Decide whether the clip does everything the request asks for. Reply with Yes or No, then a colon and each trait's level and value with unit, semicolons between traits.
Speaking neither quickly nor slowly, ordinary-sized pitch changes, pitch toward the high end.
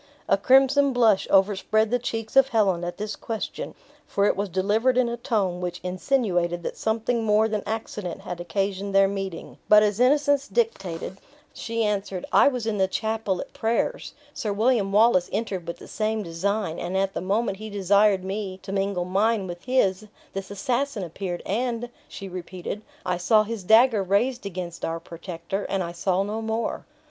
Yes: average, 180 wpm; average, 3.2 semitones; high, 205 Hz